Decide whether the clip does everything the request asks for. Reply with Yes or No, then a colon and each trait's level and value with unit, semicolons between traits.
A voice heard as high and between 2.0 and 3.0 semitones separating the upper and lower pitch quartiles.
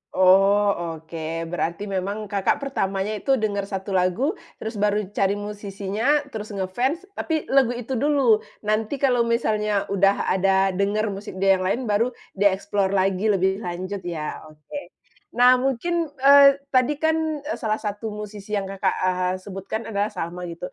No: high, 205 Hz; average, 3.6 semitones